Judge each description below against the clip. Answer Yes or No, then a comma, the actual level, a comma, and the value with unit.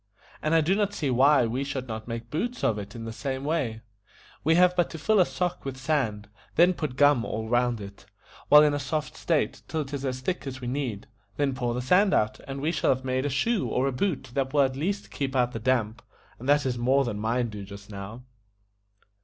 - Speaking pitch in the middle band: No, low, 130 Hz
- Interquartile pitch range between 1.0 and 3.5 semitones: No, average, 4.1 semitones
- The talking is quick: Yes, fast, 240 wpm